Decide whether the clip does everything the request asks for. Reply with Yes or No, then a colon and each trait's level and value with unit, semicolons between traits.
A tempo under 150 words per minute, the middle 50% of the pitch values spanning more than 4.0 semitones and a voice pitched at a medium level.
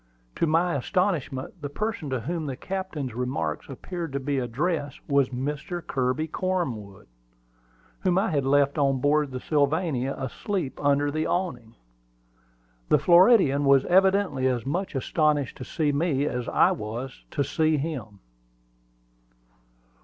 Yes: average, 140 wpm; average, 4.5 semitones; medium, 145 Hz